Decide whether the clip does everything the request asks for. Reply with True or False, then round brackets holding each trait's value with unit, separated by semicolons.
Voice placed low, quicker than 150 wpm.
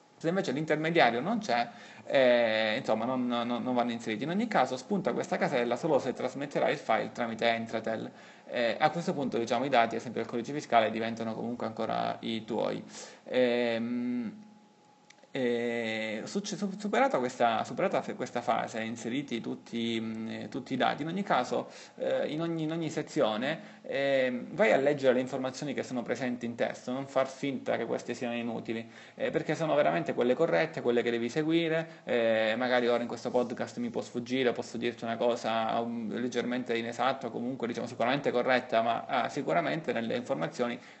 True (120 Hz; 170 wpm)